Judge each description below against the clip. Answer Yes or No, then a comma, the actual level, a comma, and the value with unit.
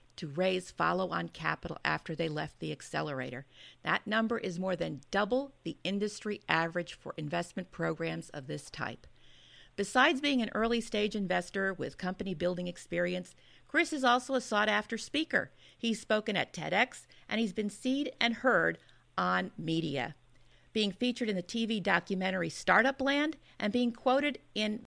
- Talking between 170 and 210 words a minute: No, average, 160 wpm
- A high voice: Yes, high, 200 Hz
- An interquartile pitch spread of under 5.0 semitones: No, wide, 5.4 semitones